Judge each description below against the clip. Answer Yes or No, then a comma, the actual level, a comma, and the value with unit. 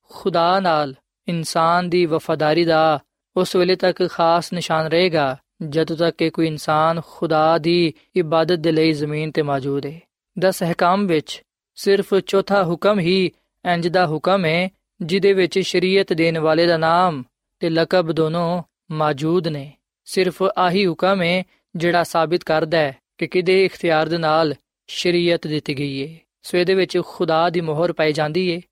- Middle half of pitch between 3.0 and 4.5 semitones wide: No, narrow, 2.4 semitones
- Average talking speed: Yes, average, 140 wpm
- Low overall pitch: No, medium, 170 Hz